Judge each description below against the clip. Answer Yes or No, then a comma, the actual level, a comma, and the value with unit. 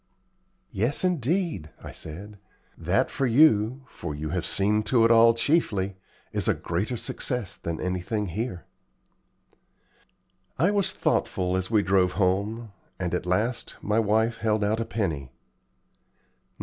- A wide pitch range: No, average, 4.1 semitones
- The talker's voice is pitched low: Yes, low, 105 Hz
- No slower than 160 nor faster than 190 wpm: No, slow, 135 wpm